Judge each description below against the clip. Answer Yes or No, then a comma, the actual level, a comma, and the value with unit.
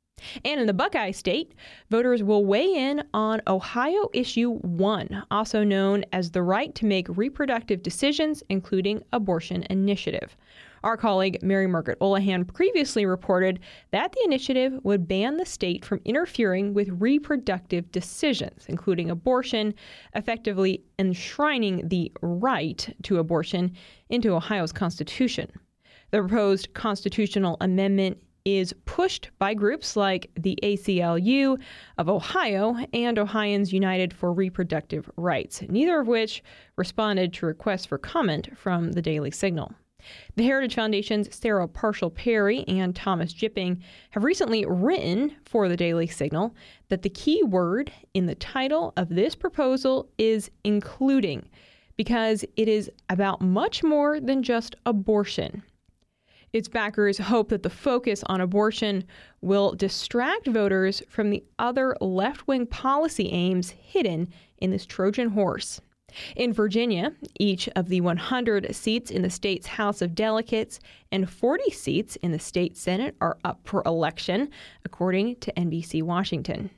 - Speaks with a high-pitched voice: Yes, high, 205 Hz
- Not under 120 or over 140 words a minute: Yes, slow, 135 wpm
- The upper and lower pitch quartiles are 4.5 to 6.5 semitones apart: No, average, 4.0 semitones